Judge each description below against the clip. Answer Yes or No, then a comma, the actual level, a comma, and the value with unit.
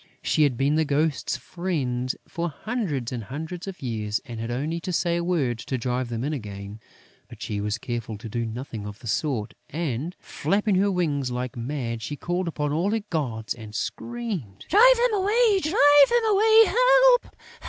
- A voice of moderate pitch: Yes, medium, 145 Hz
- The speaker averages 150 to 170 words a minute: No, average, 185 wpm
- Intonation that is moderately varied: No, wide, 8.1 semitones